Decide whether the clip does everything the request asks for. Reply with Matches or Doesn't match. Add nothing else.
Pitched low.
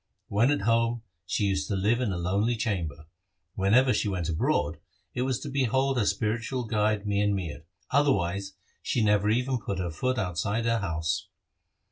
Matches